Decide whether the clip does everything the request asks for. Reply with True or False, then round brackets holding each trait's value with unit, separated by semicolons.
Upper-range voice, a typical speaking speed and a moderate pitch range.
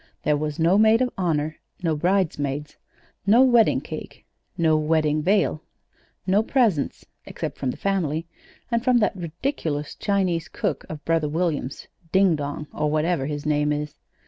False (160 Hz; 150 wpm; 4.6 semitones)